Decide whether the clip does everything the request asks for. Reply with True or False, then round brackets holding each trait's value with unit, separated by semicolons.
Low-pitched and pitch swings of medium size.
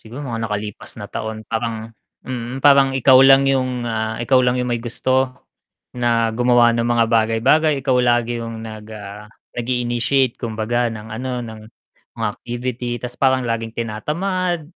False (120 Hz; 2.2 semitones)